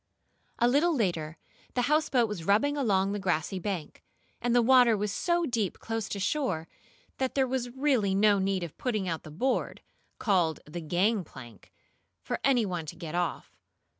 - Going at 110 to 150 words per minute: No, average, 170 wpm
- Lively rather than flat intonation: Yes, wide, 6.0 semitones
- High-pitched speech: Yes, high, 205 Hz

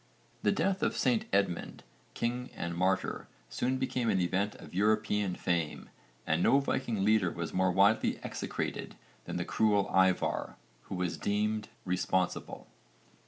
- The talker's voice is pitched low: Yes, low, 100 Hz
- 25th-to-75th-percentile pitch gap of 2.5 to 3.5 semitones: Yes, average, 3.2 semitones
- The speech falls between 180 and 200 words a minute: No, average, 140 wpm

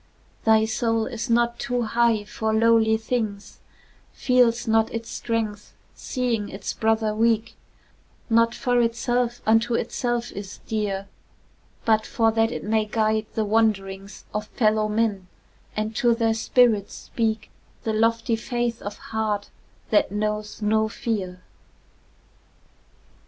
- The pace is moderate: No, slow, 125 wpm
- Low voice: No, high, 220 Hz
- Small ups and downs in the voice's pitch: Yes, narrow, 1.5 semitones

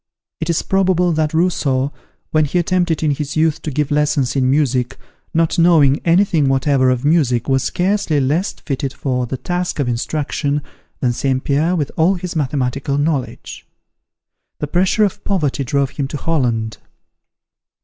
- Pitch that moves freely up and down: No, average, 3.8 semitones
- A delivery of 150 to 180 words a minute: Yes, average, 160 wpm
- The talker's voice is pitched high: No, medium, 150 Hz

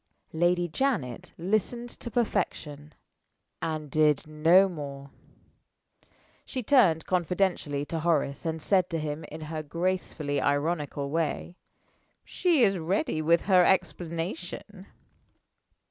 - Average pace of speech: No, slow, 110 wpm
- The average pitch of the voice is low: No, medium, 165 Hz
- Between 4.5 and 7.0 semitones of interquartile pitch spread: No, average, 3.5 semitones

